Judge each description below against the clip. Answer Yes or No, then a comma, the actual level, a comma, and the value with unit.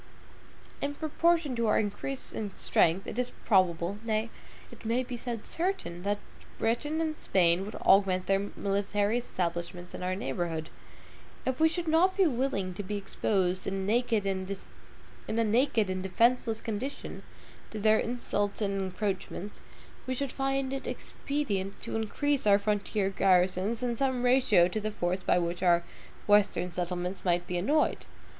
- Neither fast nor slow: Yes, average, 150 wpm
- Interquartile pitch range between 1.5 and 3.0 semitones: No, average, 4.9 semitones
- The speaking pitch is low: No, high, 205 Hz